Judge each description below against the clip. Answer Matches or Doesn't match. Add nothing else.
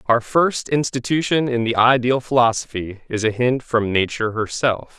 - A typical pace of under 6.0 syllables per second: Matches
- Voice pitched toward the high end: Doesn't match